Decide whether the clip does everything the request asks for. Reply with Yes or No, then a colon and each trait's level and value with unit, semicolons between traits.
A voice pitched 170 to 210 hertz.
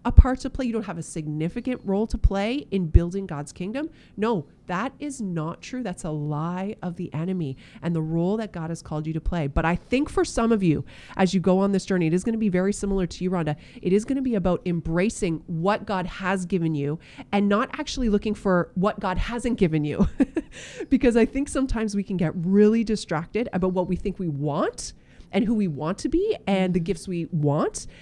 Yes: high, 190 Hz